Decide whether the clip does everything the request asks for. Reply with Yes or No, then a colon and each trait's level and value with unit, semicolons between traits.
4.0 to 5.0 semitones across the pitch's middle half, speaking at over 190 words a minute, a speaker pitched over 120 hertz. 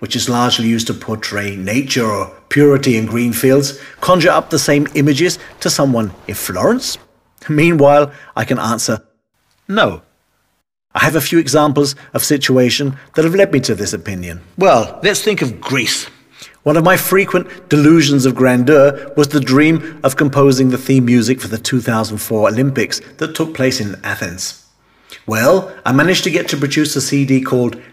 No: average, 4.4 semitones; average, 180 wpm; low, 135 Hz